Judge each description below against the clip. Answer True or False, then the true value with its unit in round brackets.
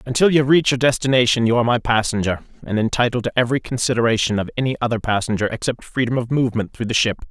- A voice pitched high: False (120 Hz)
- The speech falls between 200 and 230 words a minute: True (205 wpm)